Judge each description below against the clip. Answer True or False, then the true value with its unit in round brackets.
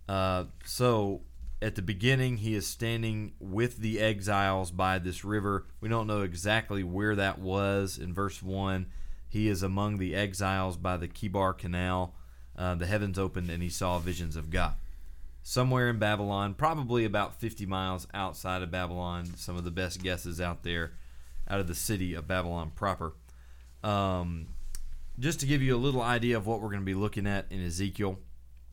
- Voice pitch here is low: True (95 Hz)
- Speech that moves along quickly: False (180 wpm)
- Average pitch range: True (3.2 semitones)